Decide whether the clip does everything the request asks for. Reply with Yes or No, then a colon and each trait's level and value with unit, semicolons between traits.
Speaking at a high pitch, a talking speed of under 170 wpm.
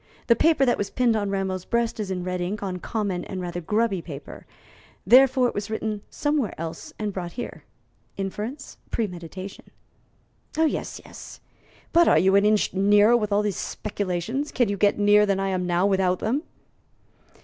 No: high, 205 Hz; average, 175 wpm